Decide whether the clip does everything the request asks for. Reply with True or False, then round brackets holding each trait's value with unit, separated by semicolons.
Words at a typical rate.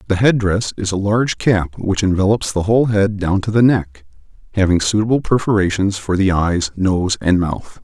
True (190 wpm)